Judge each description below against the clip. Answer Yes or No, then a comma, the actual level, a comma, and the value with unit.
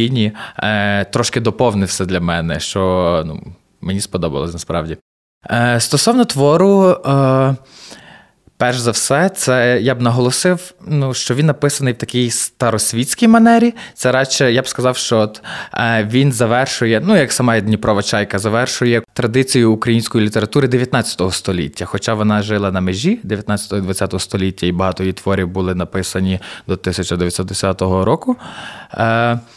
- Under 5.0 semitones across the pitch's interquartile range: No, wide, 5.4 semitones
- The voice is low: Yes, low, 115 Hz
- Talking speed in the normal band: Yes, average, 125 wpm